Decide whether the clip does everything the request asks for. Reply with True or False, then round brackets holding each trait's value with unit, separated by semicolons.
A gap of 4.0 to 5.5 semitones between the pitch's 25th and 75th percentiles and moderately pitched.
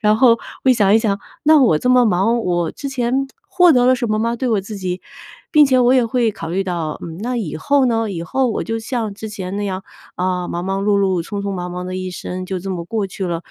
False (4.7 semitones; 205 Hz)